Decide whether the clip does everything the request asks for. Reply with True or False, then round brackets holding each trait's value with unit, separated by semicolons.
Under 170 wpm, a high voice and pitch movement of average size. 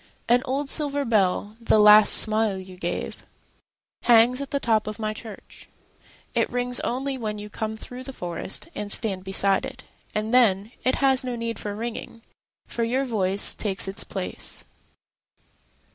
True (145 wpm; 225 Hz; 3.3 semitones)